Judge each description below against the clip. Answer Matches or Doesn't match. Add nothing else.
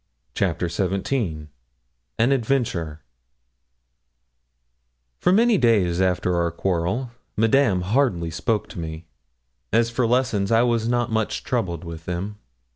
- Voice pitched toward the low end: Matches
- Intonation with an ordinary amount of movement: Doesn't match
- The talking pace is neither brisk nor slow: Doesn't match